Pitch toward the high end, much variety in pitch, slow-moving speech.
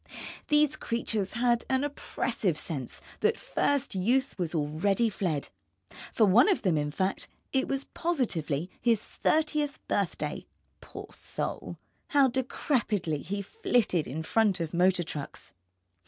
Yes: high, 210 Hz; wide, 7.6 semitones; slow, 130 wpm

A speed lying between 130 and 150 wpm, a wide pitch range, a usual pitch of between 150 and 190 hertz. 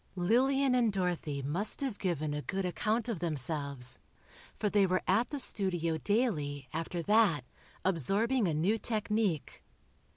Yes: average, 140 wpm; wide, 5.8 semitones; medium, 185 Hz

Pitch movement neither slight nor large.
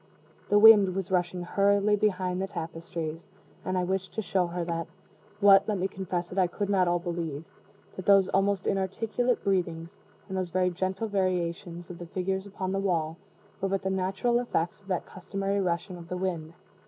No: narrow, 2.0 semitones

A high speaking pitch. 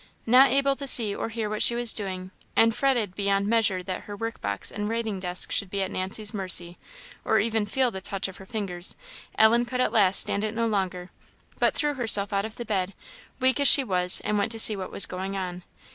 Yes: high, 210 Hz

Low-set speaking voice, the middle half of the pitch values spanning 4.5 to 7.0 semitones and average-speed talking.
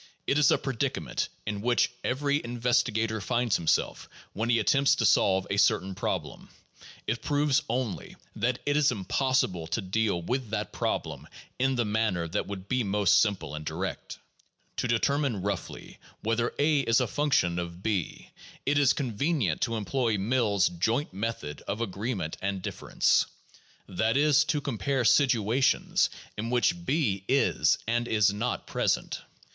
Yes: low, 115 Hz; average, 4.8 semitones; average, 155 wpm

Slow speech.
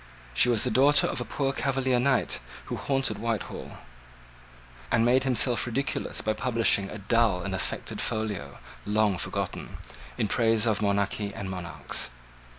No: average, 150 wpm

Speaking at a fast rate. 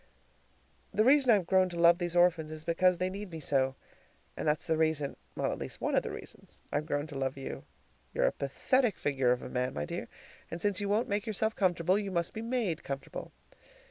Yes: fast, 215 wpm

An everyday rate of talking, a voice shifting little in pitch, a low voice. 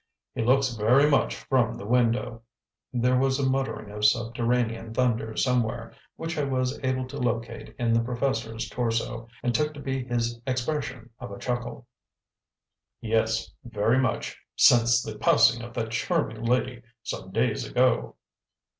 Yes: average, 150 wpm; narrow, 2.1 semitones; low, 120 Hz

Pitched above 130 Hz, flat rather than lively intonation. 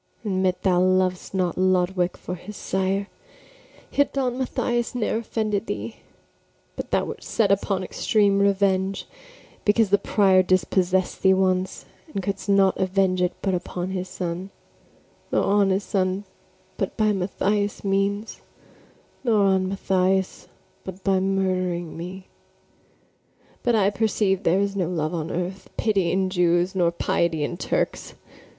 Yes: high, 190 Hz; narrow, 1.5 semitones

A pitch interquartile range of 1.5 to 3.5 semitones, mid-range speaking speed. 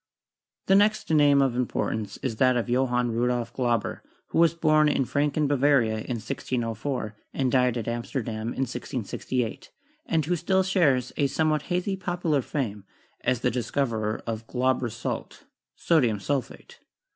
No: average, 4.2 semitones; average, 150 wpm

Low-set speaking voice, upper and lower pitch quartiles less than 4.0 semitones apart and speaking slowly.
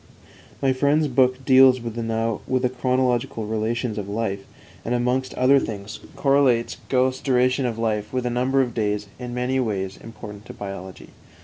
No: low, 120 Hz; average, 2.9 semitones; average, 165 wpm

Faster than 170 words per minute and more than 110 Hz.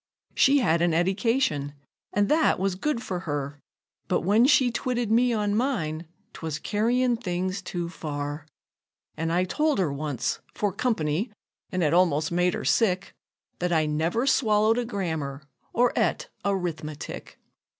No: average, 150 wpm; medium, 185 Hz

